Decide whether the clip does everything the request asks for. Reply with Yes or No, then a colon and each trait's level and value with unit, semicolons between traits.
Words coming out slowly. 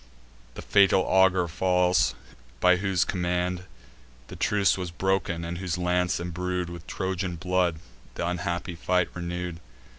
Yes: slow, 130 wpm